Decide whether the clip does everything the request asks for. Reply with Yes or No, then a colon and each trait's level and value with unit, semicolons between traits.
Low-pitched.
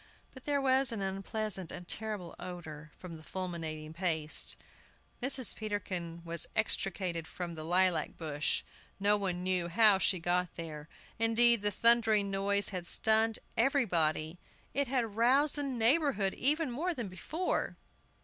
No: high, 195 Hz